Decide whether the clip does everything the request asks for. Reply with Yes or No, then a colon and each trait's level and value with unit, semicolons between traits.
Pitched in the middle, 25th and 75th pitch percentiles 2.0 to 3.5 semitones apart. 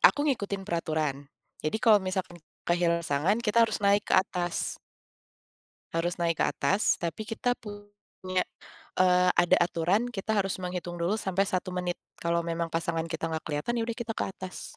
Yes: medium, 180 Hz; average, 3.2 semitones